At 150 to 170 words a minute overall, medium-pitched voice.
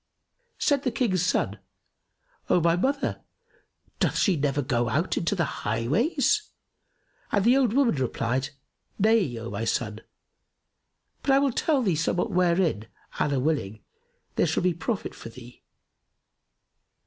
No: slow, 135 wpm; medium, 170 Hz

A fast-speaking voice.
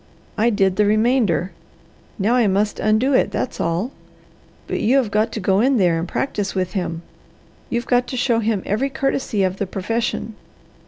No: average, 180 wpm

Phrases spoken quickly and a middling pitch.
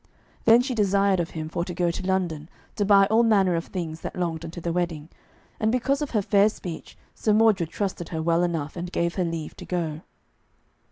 Yes: fast, 215 wpm; medium, 180 Hz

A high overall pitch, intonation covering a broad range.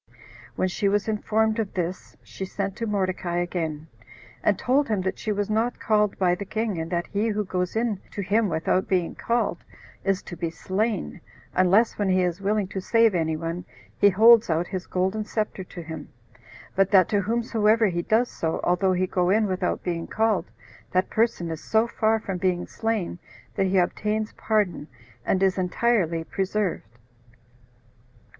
No: high, 195 Hz; average, 3.4 semitones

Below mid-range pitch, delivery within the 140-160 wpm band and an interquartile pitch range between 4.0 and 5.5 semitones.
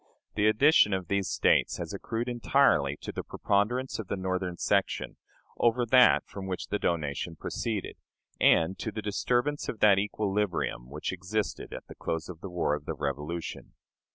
No: low, 100 Hz; average, 170 wpm; average, 4.5 semitones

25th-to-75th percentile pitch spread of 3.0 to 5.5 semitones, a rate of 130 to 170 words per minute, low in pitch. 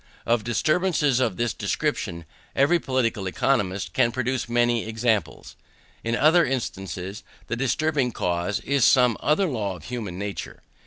Yes: average, 4.7 semitones; average, 140 wpm; low, 120 Hz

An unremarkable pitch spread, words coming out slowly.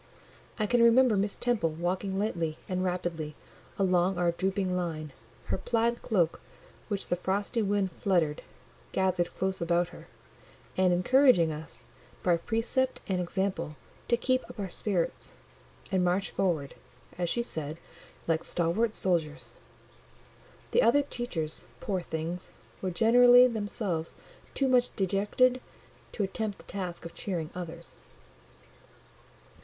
Yes: average, 4.2 semitones; slow, 130 wpm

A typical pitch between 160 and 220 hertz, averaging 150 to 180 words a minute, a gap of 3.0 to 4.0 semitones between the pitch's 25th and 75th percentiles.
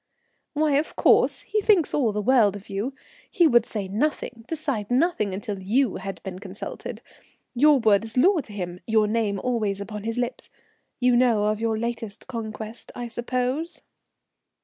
No: high, 230 Hz; average, 170 wpm; average, 3.7 semitones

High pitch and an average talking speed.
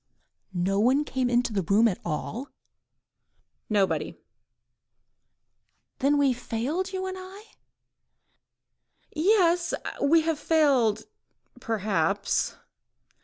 No: very high, 255 Hz; slow, 90 wpm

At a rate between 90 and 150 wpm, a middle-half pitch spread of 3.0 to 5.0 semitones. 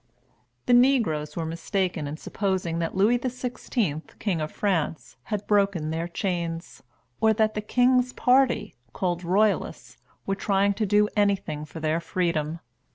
Yes: average, 145 wpm; average, 4.6 semitones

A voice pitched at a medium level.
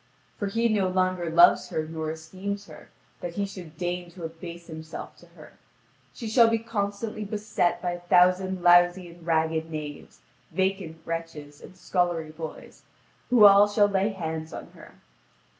Yes: medium, 175 Hz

